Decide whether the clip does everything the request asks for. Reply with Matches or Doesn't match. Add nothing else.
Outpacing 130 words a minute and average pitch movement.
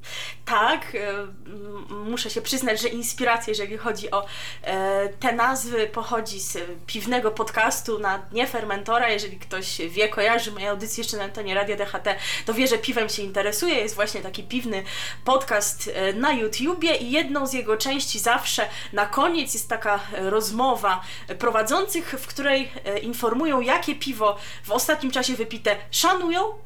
Matches